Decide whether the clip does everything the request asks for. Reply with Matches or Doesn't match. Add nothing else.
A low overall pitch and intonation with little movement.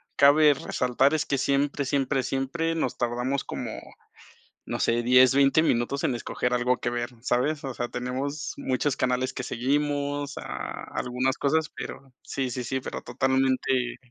Matches